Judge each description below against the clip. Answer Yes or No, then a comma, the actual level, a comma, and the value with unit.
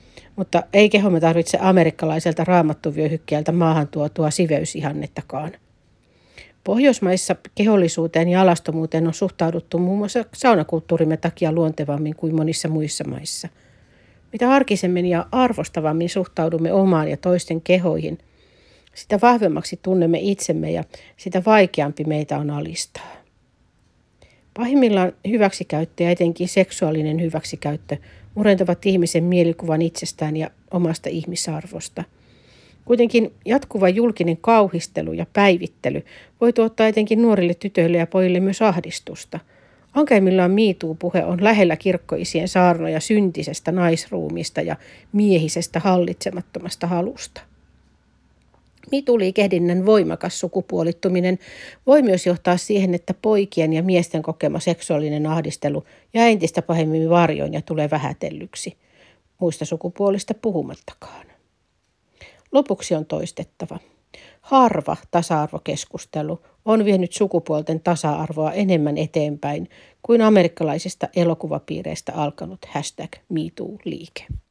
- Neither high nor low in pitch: Yes, medium, 175 Hz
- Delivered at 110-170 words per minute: No, average, 100 wpm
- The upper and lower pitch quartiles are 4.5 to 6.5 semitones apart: No, average, 3.3 semitones